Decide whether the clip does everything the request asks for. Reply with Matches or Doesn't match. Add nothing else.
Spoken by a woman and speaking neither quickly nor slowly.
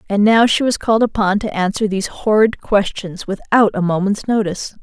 Matches